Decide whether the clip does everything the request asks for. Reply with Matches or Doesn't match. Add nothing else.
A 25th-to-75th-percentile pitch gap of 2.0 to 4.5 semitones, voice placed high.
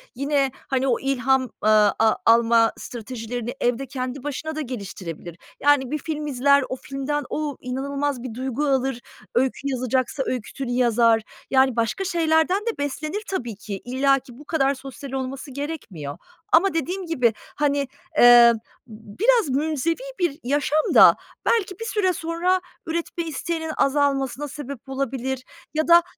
Matches